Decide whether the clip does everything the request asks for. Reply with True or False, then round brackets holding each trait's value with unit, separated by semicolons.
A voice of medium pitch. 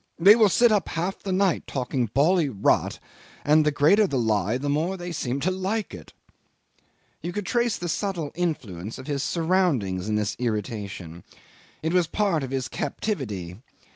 True (150 Hz)